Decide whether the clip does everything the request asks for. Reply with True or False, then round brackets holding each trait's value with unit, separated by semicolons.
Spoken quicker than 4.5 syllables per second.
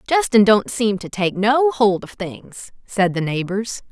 False (3.9 syllables/s)